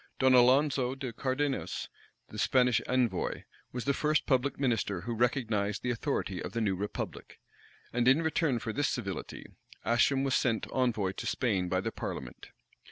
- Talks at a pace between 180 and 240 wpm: No, average, 165 wpm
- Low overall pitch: Yes, low, 125 Hz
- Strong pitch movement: No, average, 3.5 semitones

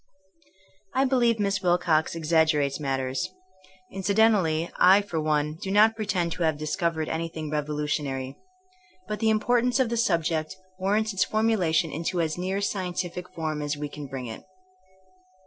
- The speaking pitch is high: No, medium, 170 Hz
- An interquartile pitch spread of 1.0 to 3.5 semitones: No, average, 4.8 semitones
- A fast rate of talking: No, average, 150 wpm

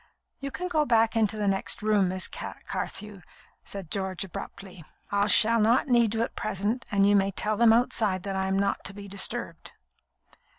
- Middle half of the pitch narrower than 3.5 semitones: Yes, narrow, 2.6 semitones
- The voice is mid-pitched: No, high, 205 Hz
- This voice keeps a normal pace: Yes, average, 185 wpm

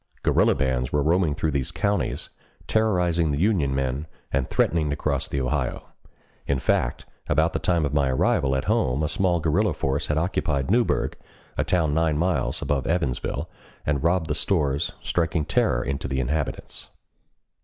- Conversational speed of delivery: Yes, average, 165 wpm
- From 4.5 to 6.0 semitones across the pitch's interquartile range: No, average, 3.8 semitones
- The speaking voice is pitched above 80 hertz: No, very low, 75 Hz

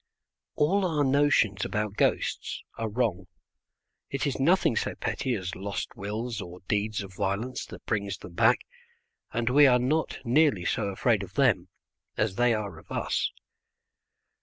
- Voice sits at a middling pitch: No, low, 115 Hz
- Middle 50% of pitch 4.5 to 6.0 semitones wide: Yes, average, 5.1 semitones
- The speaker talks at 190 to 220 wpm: No, average, 155 wpm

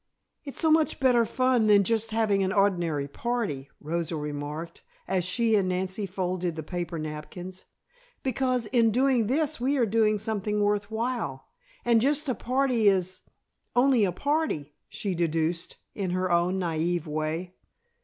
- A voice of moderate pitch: No, high, 200 Hz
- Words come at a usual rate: Yes, average, 155 wpm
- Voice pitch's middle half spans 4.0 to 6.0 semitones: Yes, wide, 5.5 semitones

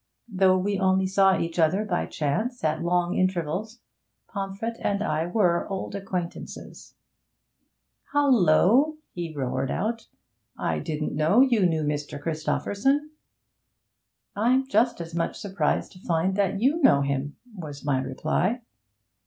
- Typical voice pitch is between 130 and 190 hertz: Yes, medium, 185 Hz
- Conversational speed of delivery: No, slow, 130 wpm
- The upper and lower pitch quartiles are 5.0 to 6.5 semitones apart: Yes, average, 5.3 semitones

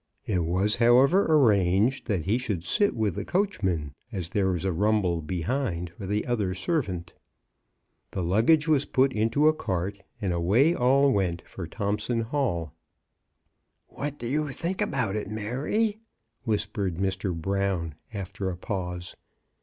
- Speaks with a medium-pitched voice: No, low, 105 Hz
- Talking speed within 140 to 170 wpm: Yes, average, 155 wpm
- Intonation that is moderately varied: No, wide, 6.2 semitones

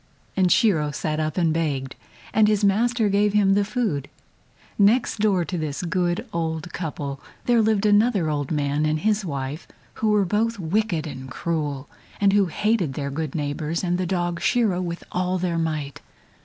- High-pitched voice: No, medium, 175 Hz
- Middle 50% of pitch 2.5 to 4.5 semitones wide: No, average, 5.1 semitones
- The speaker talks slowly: No, average, 175 wpm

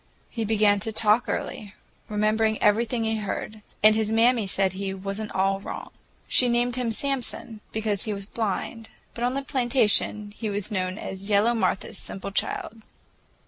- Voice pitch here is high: Yes, high, 215 Hz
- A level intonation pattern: Yes, narrow, 2.3 semitones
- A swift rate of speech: No, average, 170 wpm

